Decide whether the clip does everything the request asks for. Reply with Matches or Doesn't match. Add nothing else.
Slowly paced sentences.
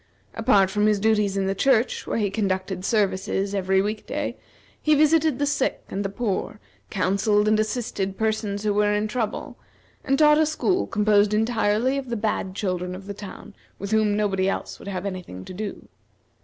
Doesn't match